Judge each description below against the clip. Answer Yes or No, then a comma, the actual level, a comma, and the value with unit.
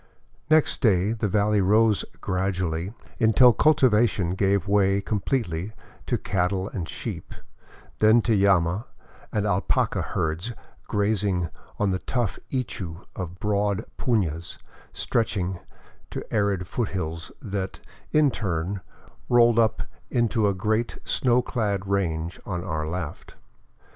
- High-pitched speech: No, low, 100 Hz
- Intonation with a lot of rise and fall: No, average, 3.5 semitones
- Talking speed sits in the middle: No, slow, 120 wpm